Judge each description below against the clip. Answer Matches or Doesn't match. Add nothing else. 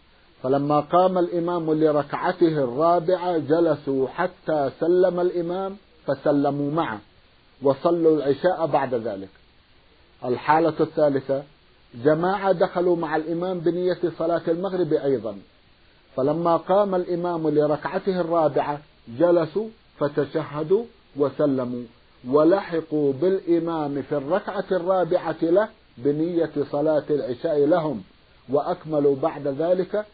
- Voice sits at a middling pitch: Matches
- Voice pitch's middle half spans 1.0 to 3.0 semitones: Doesn't match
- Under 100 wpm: Matches